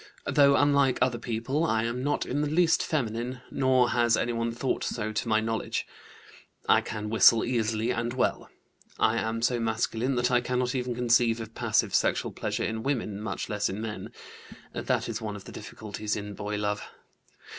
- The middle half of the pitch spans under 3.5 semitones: Yes, narrow, 2.4 semitones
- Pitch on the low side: Yes, low, 115 Hz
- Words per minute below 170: No, average, 180 wpm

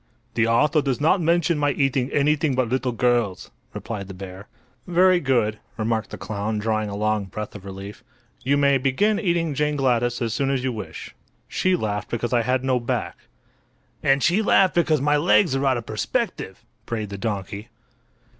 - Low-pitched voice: Yes, low, 125 Hz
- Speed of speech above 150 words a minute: Yes, average, 185 wpm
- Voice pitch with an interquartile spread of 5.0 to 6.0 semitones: Yes, average, 5.3 semitones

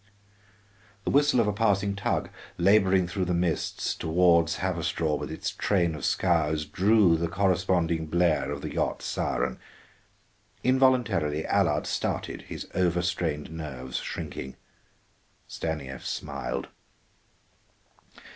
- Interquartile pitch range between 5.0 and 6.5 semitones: No, average, 3.6 semitones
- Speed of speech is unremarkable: No, slow, 115 wpm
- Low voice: Yes, very low, 85 Hz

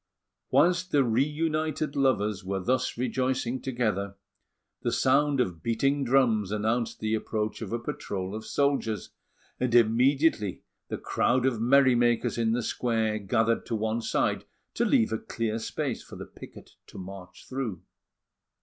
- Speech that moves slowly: No, average, 150 wpm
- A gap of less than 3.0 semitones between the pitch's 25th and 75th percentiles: No, average, 3.5 semitones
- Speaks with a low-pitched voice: Yes, low, 115 Hz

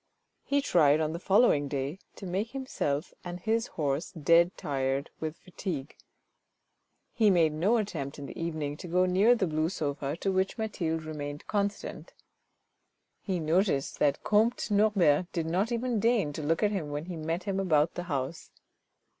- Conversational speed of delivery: Yes, average, 170 wpm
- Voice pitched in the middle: Yes, medium, 170 Hz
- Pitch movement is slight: No, average, 5.0 semitones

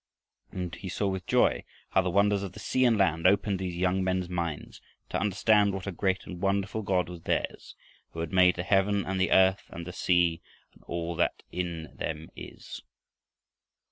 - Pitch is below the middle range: Yes, very low, 95 Hz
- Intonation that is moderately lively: No, narrow, 2.0 semitones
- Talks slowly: No, average, 195 wpm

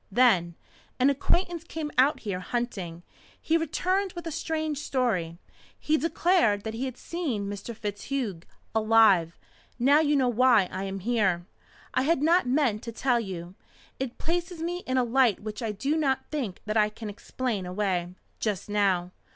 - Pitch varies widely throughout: Yes, wide, 6.5 semitones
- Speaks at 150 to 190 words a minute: Yes, average, 165 wpm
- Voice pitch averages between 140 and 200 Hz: No, high, 240 Hz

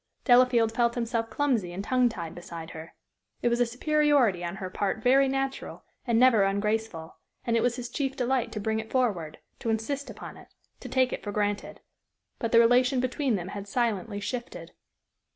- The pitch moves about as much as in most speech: Yes, average, 3.7 semitones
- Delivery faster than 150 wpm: Yes, average, 190 wpm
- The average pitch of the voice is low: No, high, 230 Hz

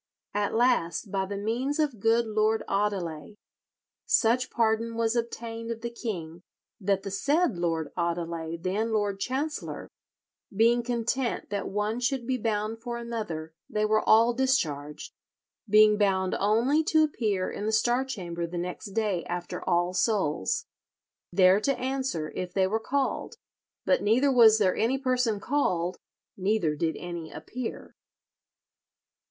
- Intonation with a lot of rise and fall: No, average, 4.4 semitones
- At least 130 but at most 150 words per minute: Yes, average, 145 wpm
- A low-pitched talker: No, high, 215 Hz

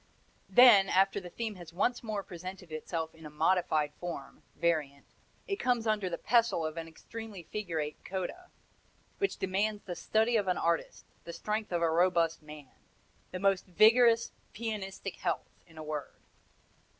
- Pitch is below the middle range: No, medium, 185 Hz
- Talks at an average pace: Yes, average, 160 wpm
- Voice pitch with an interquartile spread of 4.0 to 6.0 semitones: Yes, average, 4.6 semitones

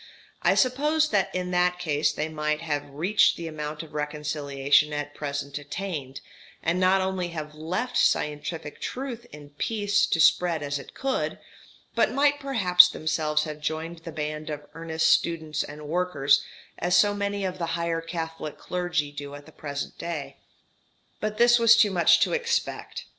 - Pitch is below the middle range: No, medium, 165 Hz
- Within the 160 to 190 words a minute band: Yes, average, 165 wpm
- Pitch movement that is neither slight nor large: Yes, average, 3.9 semitones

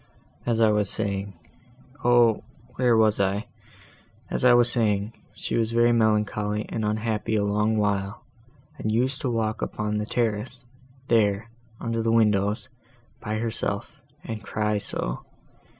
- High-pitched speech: No, low, 110 Hz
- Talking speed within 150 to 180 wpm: No, slow, 135 wpm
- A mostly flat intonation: Yes, narrow, 1.9 semitones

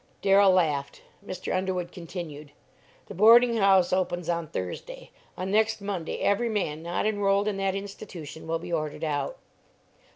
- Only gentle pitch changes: No, average, 3.6 semitones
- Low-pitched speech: No, medium, 185 Hz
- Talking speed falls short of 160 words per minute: Yes, average, 150 wpm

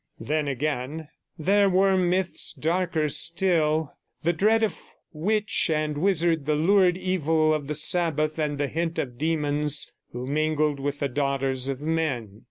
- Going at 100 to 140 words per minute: No, average, 150 wpm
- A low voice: No, medium, 155 Hz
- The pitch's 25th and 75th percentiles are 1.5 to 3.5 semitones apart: Yes, average, 3.1 semitones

